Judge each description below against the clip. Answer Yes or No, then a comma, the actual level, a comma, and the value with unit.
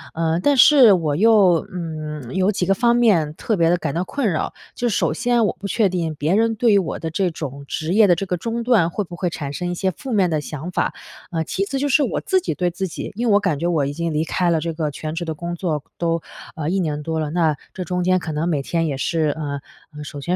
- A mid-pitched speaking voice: Yes, medium, 175 Hz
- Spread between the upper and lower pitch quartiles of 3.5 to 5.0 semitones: Yes, average, 4.1 semitones